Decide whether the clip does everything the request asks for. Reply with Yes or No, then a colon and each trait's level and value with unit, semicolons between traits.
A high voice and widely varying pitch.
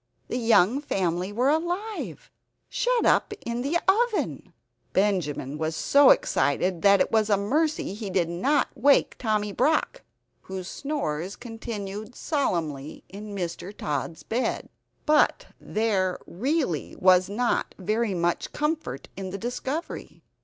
Yes: high, 210 Hz; wide, 7.3 semitones